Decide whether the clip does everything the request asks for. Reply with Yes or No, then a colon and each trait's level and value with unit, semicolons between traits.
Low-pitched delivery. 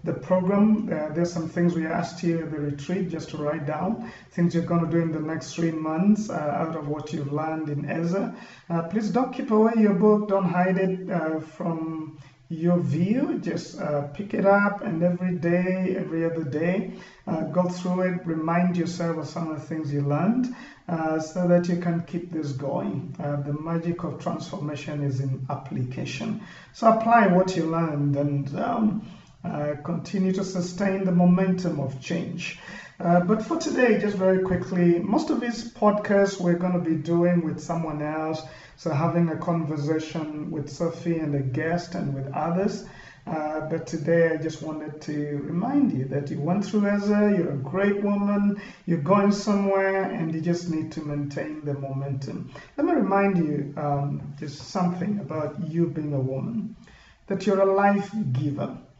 No: medium, 170 Hz